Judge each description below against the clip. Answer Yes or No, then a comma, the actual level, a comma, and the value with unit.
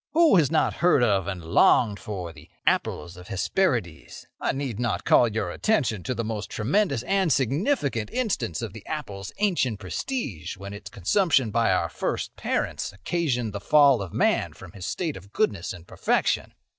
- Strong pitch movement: Yes, wide, 7.4 semitones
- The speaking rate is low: No, average, 180 wpm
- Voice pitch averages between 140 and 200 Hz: No, low, 110 Hz